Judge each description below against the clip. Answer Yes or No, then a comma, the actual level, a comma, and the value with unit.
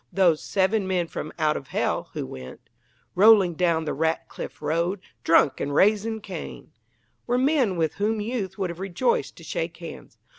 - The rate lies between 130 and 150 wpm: No, average, 170 wpm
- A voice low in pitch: No, high, 190 Hz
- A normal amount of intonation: Yes, average, 4.7 semitones